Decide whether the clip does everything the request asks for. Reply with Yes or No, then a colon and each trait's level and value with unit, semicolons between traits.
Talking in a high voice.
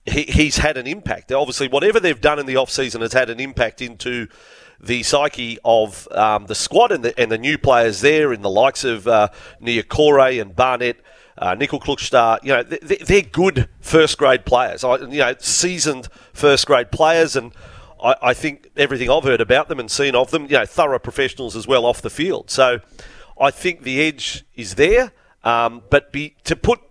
No: low, 135 Hz